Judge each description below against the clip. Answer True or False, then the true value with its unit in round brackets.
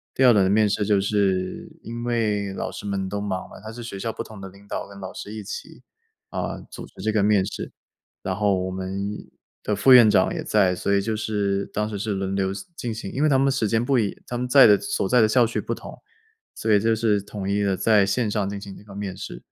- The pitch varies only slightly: True (2.3 semitones)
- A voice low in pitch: True (105 Hz)